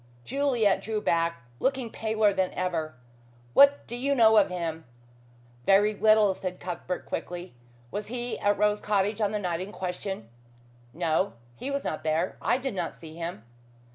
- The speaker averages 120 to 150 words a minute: No, average, 165 wpm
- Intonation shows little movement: No, average, 3.9 semitones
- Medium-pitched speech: No, high, 200 Hz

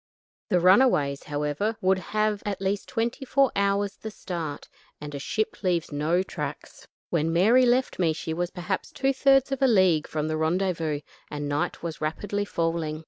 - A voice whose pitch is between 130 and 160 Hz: No, medium, 185 Hz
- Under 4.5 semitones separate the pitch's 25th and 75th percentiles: No, average, 5.2 semitones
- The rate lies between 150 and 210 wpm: Yes, average, 175 wpm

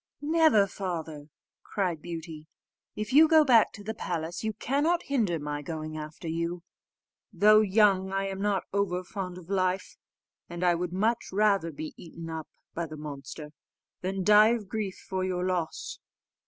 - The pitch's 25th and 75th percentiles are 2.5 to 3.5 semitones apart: No, average, 4.1 semitones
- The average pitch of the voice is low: No, medium, 185 Hz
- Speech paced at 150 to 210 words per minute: Yes, average, 165 wpm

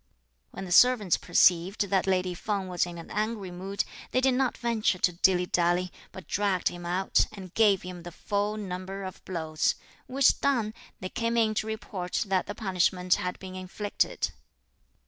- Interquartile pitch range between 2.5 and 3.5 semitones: Yes, average, 2.9 semitones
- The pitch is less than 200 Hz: Yes, high, 190 Hz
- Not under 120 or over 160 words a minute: No, average, 175 wpm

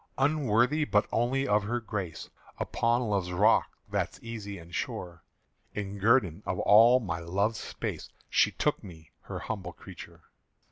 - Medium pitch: No, low, 105 Hz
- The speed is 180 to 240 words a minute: No, average, 145 wpm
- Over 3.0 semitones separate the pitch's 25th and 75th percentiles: Yes, average, 4.5 semitones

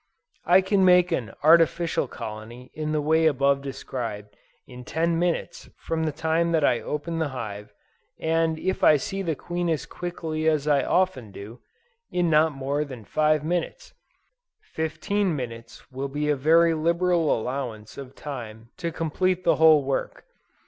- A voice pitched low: No, medium, 155 Hz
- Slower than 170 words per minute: Yes, average, 160 wpm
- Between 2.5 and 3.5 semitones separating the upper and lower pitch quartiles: No, average, 4.1 semitones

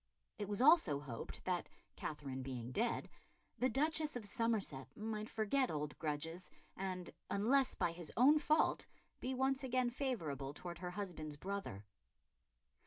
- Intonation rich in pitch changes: Yes, wide, 8.8 semitones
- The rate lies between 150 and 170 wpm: No, average, 140 wpm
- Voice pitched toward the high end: Yes, high, 200 Hz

